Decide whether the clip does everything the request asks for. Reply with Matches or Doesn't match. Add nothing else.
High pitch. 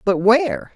Matches